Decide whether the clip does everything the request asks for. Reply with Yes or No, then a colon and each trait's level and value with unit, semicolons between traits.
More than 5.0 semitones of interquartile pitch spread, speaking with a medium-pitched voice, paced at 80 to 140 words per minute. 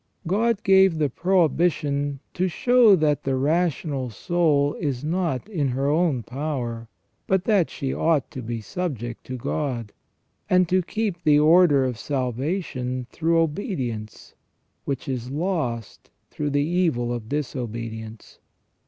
Yes: wide, 5.6 semitones; medium, 145 Hz; slow, 135 wpm